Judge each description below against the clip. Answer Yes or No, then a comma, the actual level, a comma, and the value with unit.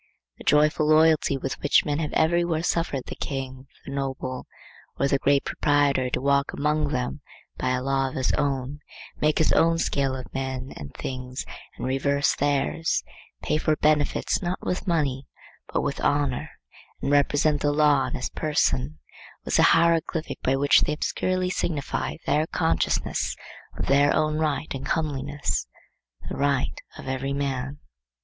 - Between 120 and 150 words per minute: No, average, 160 wpm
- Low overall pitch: No, medium, 145 Hz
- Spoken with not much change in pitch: Yes, narrow, 2.3 semitones